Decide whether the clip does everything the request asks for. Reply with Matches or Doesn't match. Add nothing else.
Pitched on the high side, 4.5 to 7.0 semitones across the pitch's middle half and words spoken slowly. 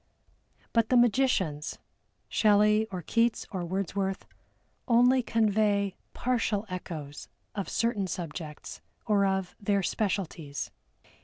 Doesn't match